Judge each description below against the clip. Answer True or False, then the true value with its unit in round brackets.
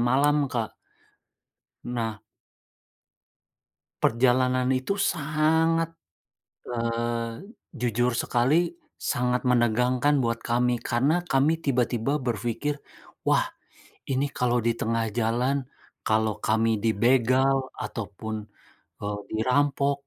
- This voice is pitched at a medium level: False (125 Hz)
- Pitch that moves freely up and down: False (2.9 semitones)